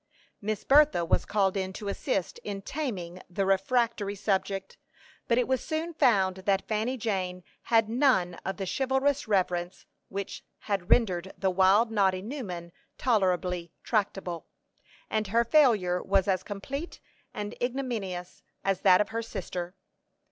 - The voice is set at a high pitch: Yes, high, 200 Hz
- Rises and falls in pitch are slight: No, average, 3.9 semitones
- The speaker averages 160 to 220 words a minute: No, average, 140 wpm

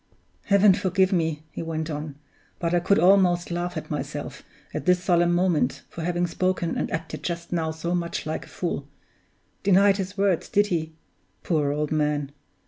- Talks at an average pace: Yes, average, 175 wpm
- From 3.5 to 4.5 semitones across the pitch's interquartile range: No, narrow, 2.5 semitones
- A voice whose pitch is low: No, medium, 175 Hz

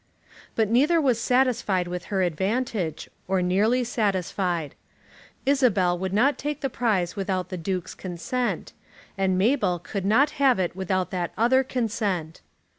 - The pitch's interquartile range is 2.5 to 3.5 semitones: No, wide, 5.4 semitones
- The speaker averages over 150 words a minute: No, average, 140 wpm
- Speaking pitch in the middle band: No, high, 200 Hz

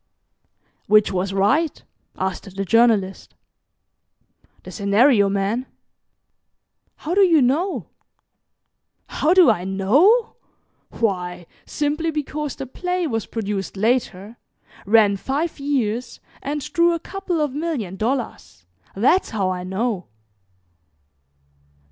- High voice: Yes, high, 235 Hz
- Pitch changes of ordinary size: No, wide, 7.4 semitones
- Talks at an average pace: No, slow, 110 wpm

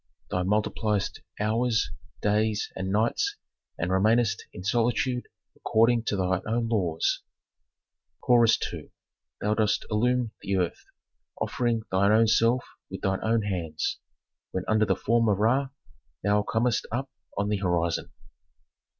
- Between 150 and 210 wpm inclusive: No, slow, 135 wpm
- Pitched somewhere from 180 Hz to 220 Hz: No, low, 110 Hz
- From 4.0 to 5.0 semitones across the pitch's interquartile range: No, average, 3.1 semitones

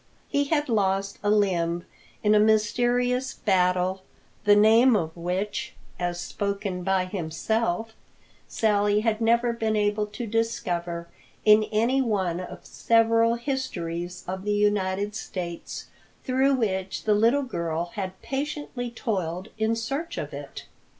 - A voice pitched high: Yes, high, 210 Hz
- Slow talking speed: Yes, slow, 130 wpm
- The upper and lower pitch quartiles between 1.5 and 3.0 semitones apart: No, average, 3.8 semitones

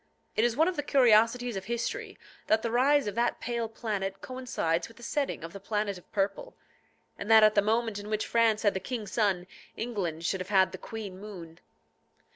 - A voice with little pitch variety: No, average, 3.3 semitones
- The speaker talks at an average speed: No, fast, 210 wpm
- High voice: Yes, high, 215 Hz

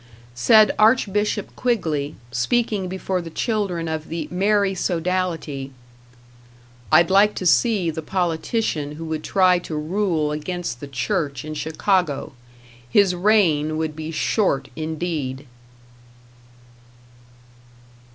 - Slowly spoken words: Yes, slow, 110 wpm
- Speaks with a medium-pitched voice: Yes, medium, 170 Hz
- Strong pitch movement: No, average, 4.2 semitones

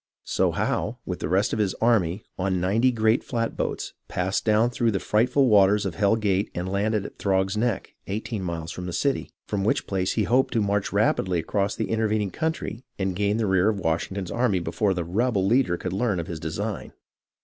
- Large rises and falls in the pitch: No, average, 3.1 semitones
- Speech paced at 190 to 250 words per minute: Yes, fast, 205 wpm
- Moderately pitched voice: No, low, 100 Hz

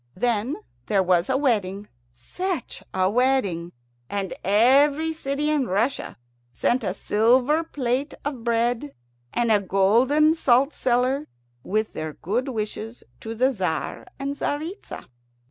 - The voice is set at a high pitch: Yes, high, 240 Hz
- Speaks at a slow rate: Yes, slow, 130 wpm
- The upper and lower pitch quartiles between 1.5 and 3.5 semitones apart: No, average, 5.3 semitones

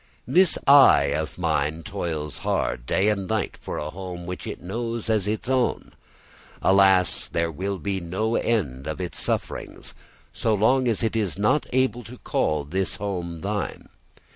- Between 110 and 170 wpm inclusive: Yes, average, 165 wpm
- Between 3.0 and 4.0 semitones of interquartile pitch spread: No, average, 4.8 semitones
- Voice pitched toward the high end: No, very low, 95 Hz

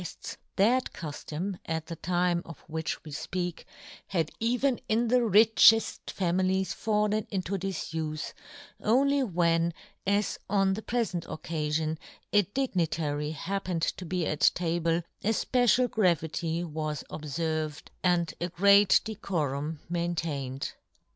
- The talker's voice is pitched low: No, medium, 175 Hz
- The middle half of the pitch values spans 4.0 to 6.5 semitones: Yes, average, 4.3 semitones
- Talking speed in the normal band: No, slow, 130 wpm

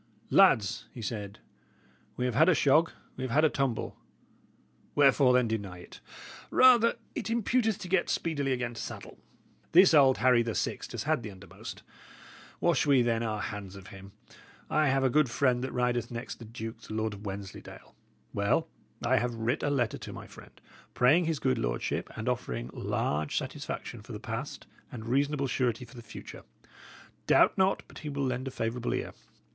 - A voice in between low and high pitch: No, low, 125 Hz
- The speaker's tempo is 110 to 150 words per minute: No, average, 185 wpm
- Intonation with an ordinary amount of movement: Yes, average, 4.2 semitones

